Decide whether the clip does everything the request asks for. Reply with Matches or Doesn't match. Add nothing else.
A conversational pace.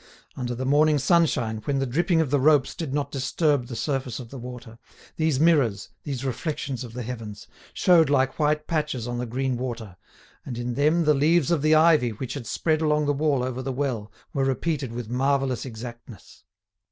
Matches